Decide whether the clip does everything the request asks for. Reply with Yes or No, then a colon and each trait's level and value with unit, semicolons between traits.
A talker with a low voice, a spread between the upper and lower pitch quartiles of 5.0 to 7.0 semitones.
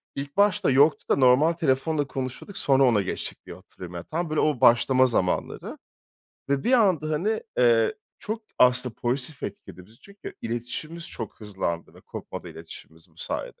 Yes: low, 130 Hz; wide, 5.5 semitones